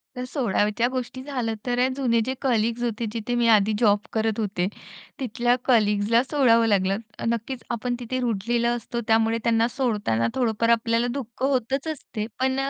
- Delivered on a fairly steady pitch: Yes, narrow, 2.3 semitones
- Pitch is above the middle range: Yes, high, 235 Hz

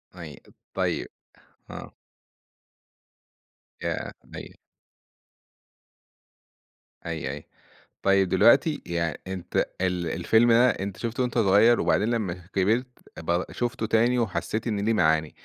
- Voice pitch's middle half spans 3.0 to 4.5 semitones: No, average, 5.0 semitones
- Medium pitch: No, low, 100 Hz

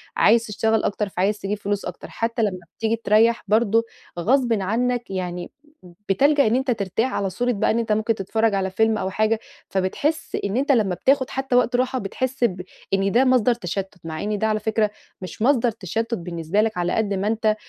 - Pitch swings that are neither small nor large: Yes, average, 3.4 semitones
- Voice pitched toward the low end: No, high, 220 Hz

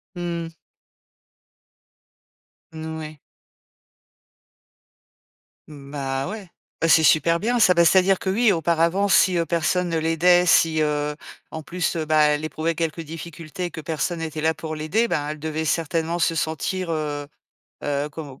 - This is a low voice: No, medium, 160 Hz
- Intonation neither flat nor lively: No, narrow, 2.1 semitones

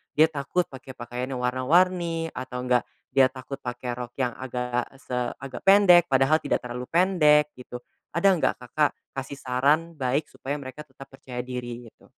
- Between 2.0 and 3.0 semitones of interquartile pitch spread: No, average, 3.6 semitones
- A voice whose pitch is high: No, low, 135 Hz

